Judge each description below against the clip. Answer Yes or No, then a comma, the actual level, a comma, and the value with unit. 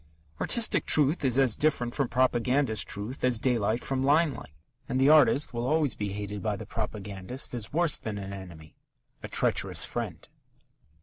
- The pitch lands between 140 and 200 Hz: No, low, 120 Hz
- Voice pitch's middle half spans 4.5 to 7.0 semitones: Yes, average, 4.9 semitones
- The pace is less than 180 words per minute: Yes, average, 165 wpm